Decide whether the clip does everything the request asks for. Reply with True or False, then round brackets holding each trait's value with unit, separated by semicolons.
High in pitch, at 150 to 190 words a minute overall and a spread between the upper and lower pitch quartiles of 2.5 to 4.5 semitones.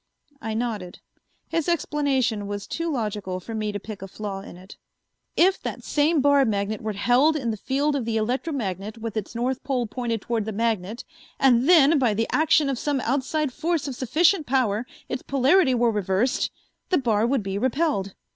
False (240 Hz; 185 wpm; 5.0 semitones)